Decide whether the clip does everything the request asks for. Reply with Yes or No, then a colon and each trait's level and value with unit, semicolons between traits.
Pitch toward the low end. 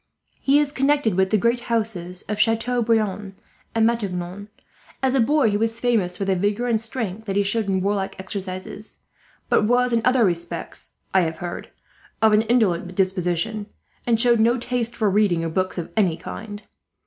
No: high, 210 Hz